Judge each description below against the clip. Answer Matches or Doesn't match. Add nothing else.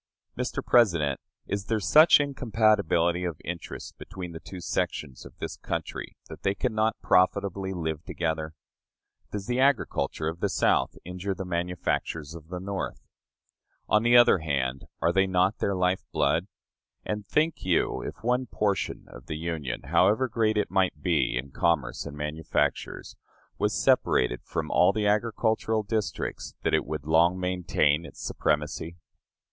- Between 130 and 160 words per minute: Matches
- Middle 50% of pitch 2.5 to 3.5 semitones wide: Doesn't match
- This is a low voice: Matches